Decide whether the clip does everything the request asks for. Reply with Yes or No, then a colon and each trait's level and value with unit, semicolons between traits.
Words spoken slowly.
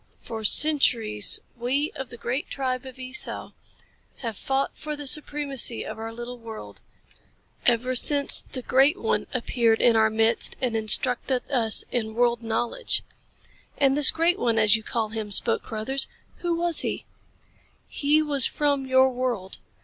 No: average, 155 wpm